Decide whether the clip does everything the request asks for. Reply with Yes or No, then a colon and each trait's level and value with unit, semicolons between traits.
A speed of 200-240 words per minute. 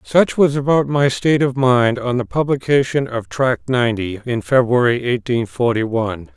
No: average, 170 wpm